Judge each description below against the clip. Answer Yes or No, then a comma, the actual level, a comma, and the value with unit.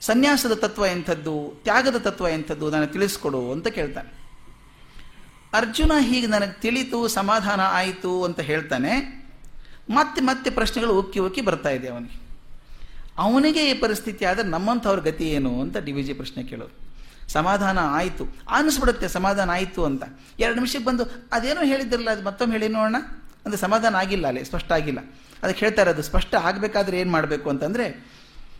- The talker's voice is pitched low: No, high, 195 Hz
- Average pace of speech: No, fast, 145 wpm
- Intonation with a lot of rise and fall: Yes, wide, 6.8 semitones